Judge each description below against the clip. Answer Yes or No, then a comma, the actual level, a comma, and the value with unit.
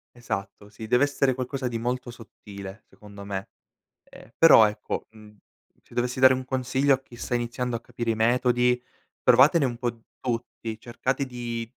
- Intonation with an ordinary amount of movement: No, narrow, 2.3 semitones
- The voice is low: Yes, low, 120 Hz